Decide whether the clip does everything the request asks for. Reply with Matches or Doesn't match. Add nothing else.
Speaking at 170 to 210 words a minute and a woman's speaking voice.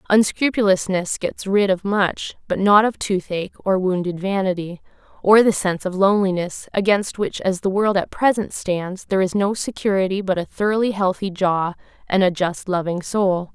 Matches